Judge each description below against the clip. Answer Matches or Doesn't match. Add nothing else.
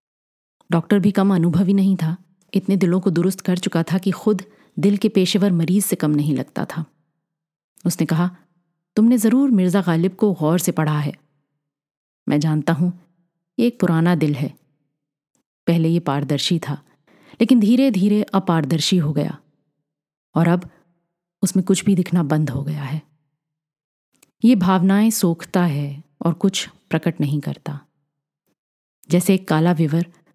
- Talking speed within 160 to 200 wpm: Doesn't match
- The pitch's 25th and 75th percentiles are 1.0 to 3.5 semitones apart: Doesn't match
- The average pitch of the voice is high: Doesn't match